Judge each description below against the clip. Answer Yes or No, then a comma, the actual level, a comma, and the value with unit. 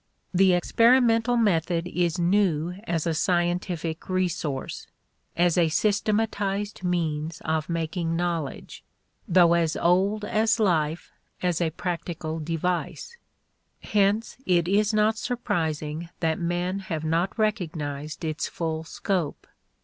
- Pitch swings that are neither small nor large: Yes, average, 3.5 semitones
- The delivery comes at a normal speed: No, slow, 115 wpm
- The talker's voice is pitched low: No, medium, 175 Hz